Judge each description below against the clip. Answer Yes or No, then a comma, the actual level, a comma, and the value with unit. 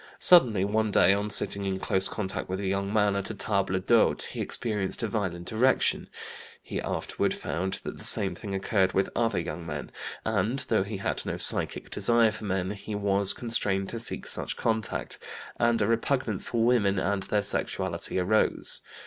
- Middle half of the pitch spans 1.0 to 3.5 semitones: Yes, narrow, 2.5 semitones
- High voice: No, low, 100 Hz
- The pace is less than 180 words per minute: No, average, 185 wpm